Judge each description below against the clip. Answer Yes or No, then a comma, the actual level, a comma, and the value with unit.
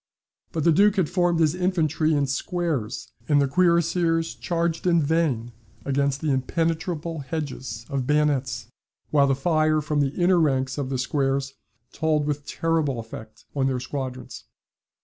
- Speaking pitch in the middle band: Yes, medium, 150 Hz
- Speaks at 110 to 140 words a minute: No, average, 150 wpm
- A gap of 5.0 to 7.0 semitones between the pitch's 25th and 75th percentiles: No, average, 3.5 semitones